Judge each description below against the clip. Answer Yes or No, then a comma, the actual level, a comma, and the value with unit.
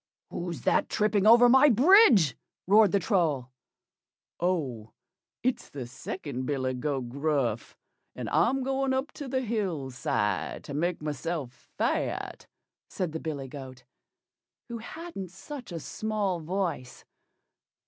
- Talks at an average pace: No, slow, 130 wpm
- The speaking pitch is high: No, medium, 175 Hz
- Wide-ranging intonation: Yes, wide, 8.8 semitones